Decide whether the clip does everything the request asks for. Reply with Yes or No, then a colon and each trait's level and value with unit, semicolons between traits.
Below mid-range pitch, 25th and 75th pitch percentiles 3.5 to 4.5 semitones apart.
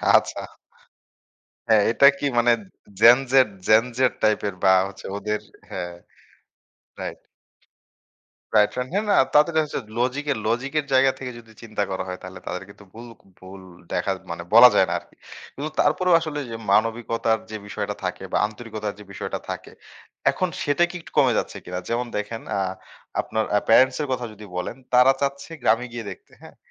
Yes: low, 115 Hz; average, 4.1 semitones